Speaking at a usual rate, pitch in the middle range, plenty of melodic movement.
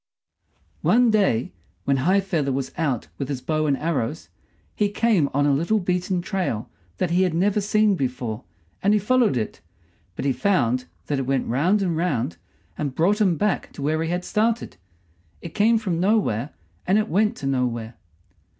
Yes: average, 180 wpm; medium, 170 Hz; wide, 7.0 semitones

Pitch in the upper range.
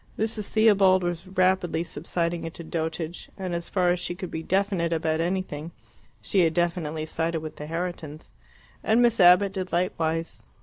No: medium, 175 Hz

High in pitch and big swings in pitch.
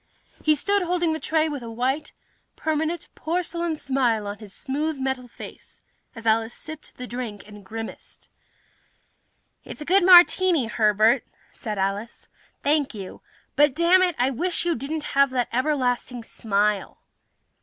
Yes: very high, 265 Hz; wide, 5.8 semitones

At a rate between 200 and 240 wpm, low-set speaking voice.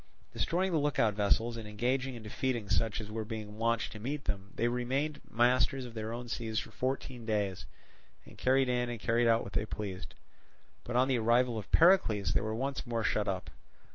Yes: fast, 205 wpm; low, 115 Hz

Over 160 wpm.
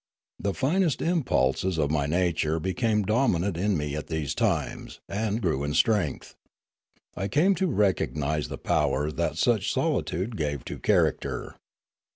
No: average, 145 wpm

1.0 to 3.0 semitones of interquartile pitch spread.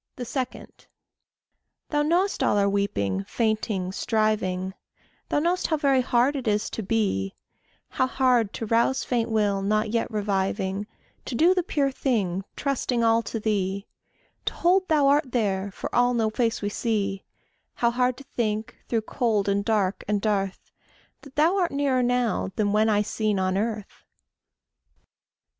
No: average, 4.1 semitones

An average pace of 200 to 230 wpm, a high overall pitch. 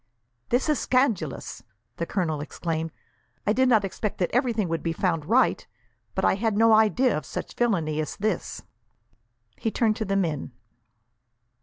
No: average, 160 wpm; high, 200 Hz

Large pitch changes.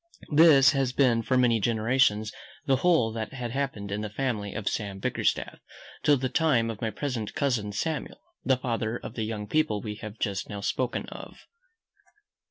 No: average, 3.9 semitones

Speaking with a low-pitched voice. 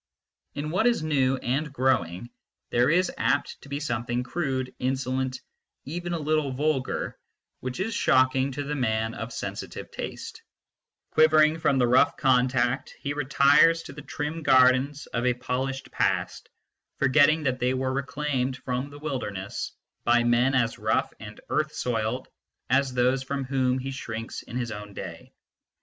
Yes: low, 130 Hz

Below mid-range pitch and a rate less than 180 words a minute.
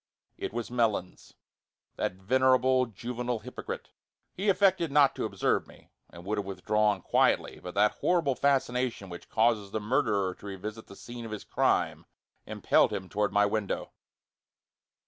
Yes: low, 110 Hz; average, 150 wpm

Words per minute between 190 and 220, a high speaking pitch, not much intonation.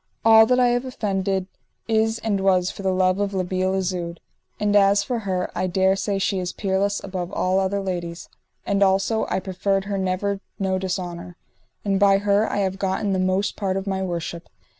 Yes: average, 200 wpm; high, 195 Hz; narrow, 1.4 semitones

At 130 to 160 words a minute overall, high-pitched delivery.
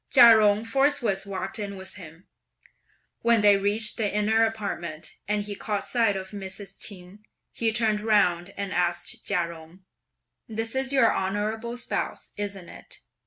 Yes: average, 155 wpm; high, 205 Hz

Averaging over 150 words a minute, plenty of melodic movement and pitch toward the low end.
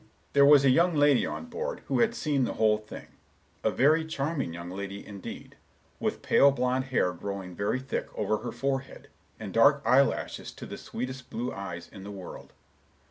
Yes: average, 180 wpm; wide, 5.8 semitones; low, 130 Hz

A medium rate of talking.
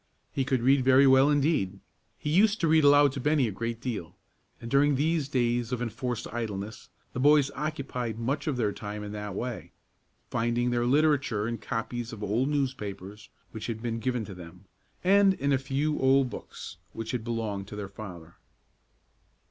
Yes: average, 180 wpm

